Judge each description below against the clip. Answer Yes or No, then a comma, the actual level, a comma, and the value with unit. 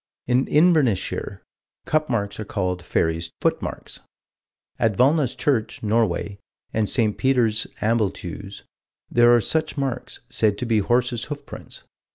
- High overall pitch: No, low, 115 Hz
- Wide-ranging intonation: No, average, 4.1 semitones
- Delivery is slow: Yes, slow, 130 wpm